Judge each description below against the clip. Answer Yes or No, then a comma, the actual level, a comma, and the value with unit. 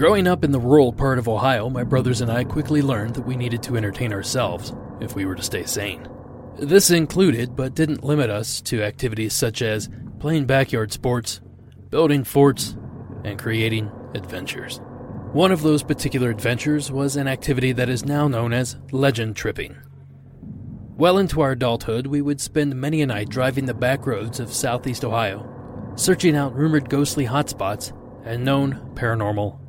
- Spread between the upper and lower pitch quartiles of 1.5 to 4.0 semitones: Yes, average, 3.5 semitones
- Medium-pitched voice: No, low, 125 Hz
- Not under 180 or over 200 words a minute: No, average, 170 wpm